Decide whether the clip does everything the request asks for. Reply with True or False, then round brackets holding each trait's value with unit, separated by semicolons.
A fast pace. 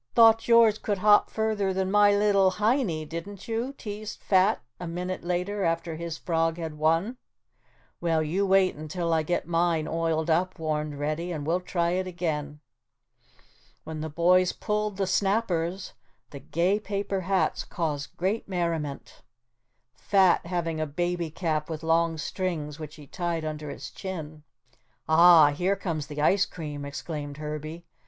False (155 wpm)